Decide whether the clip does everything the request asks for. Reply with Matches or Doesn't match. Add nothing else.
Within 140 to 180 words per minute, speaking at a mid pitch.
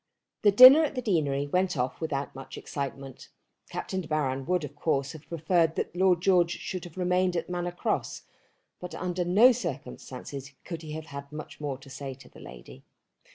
Doesn't match